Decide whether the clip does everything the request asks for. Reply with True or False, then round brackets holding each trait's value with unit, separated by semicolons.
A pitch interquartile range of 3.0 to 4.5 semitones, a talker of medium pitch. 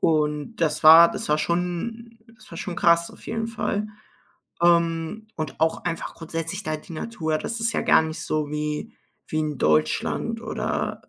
True (3.8 semitones; 165 Hz)